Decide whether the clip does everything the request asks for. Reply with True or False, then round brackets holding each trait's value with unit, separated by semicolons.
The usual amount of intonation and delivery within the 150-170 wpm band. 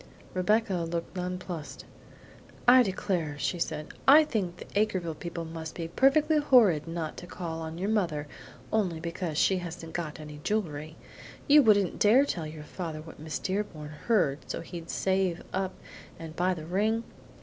True (4.1 semitones; 160 wpm)